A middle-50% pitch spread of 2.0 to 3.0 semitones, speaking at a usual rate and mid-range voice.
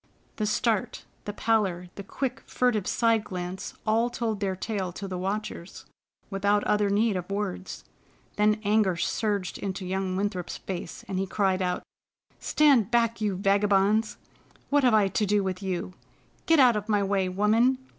No: narrow, 2.5 semitones; average, 165 wpm; high, 205 Hz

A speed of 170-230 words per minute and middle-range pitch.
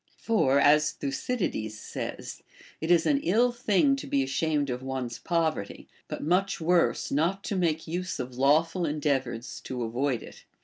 No: average, 160 wpm; medium, 155 Hz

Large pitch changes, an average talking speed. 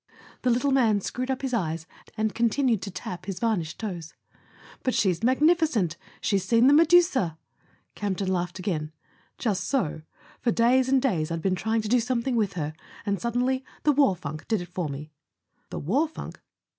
Yes: wide, 6.2 semitones; average, 180 wpm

